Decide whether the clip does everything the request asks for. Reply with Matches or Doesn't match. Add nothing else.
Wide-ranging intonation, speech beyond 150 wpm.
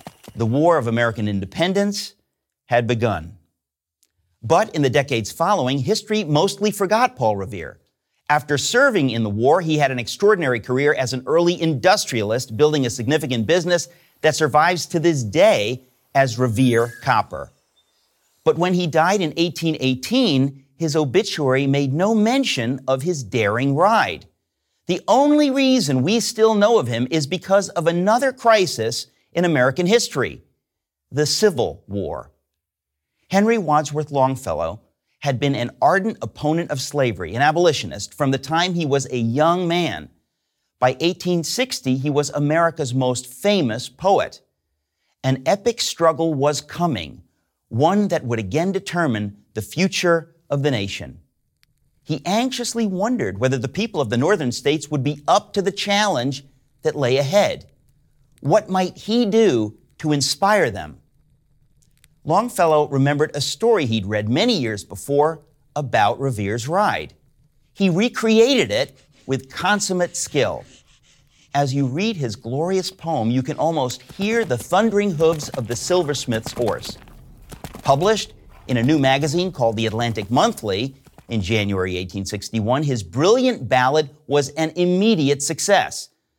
Doesn't match